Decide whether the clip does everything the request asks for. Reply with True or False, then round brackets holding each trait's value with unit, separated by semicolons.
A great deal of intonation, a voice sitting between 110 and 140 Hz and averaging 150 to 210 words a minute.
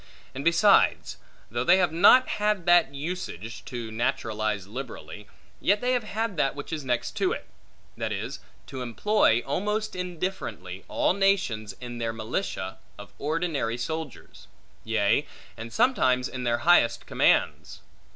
False (8.2 semitones; 135 Hz; 140 wpm)